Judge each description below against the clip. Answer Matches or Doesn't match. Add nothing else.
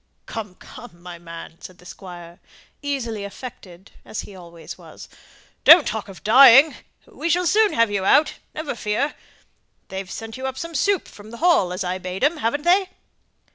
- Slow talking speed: Doesn't match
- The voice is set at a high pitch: Matches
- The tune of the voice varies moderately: Doesn't match